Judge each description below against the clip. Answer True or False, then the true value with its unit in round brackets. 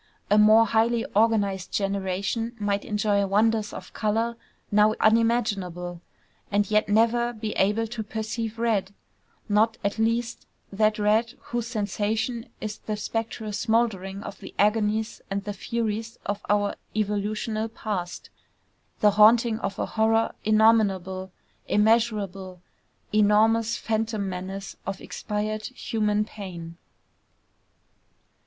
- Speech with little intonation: True (1.9 semitones)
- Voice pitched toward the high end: True (215 Hz)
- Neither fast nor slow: False (115 wpm)